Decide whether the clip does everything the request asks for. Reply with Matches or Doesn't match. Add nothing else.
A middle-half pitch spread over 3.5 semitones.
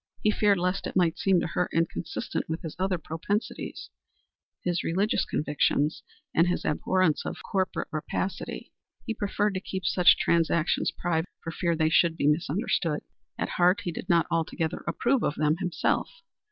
Doesn't match